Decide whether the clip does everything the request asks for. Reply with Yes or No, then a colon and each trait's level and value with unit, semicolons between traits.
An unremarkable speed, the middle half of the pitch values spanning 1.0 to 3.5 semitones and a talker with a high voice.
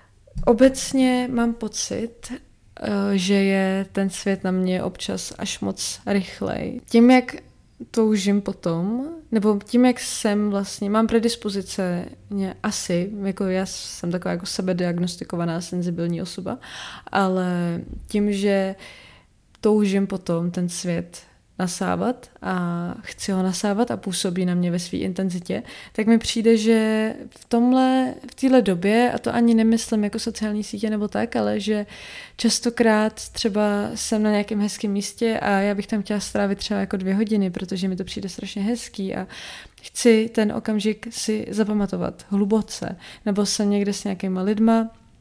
Yes: average, 145 wpm; average, 2.9 semitones; high, 205 Hz